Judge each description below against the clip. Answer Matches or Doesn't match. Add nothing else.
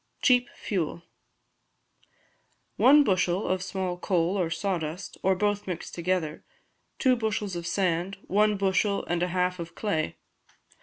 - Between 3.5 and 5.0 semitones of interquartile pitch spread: Doesn't match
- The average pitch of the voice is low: Doesn't match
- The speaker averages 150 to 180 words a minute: Doesn't match